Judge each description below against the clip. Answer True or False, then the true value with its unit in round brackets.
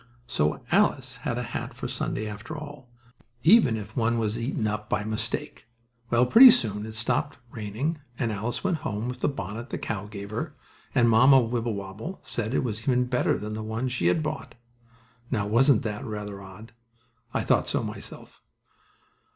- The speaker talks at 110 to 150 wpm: False (175 wpm)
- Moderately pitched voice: False (115 Hz)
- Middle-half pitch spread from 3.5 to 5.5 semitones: False (3.0 semitones)